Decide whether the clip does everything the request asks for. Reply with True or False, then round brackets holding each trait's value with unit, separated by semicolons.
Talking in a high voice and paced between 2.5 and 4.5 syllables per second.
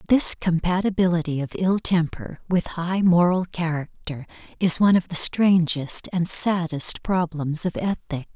False (175 Hz; 4.3 syllables/s)